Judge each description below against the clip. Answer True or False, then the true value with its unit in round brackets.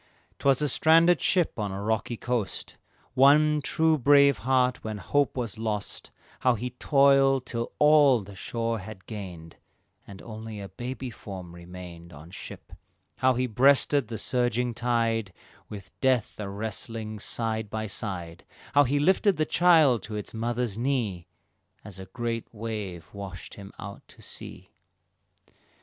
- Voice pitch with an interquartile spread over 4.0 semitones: True (4.9 semitones)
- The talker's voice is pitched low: True (115 Hz)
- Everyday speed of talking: True (150 wpm)